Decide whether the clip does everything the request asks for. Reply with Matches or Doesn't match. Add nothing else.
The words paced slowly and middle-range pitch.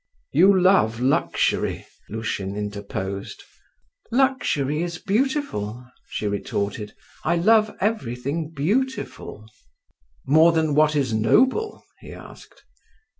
Matches